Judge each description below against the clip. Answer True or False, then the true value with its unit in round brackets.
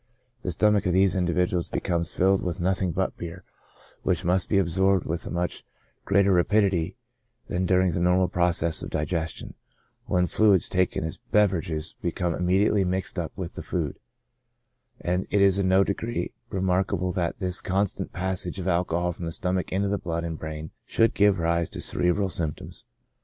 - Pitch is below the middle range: True (90 Hz)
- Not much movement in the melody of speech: True (2.1 semitones)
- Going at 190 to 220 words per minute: False (170 wpm)